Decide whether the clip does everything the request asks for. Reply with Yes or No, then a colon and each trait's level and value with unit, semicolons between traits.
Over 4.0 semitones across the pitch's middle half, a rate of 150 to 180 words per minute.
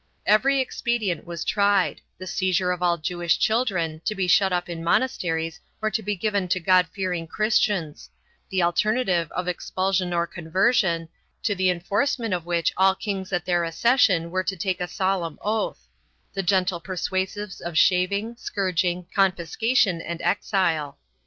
No: average, 2.8 semitones; average, 165 wpm